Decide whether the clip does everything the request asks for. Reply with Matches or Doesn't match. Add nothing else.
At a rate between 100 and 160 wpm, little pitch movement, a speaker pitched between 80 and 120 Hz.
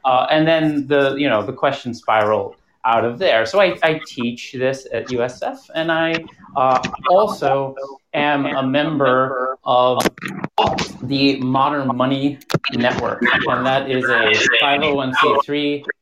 Doesn't match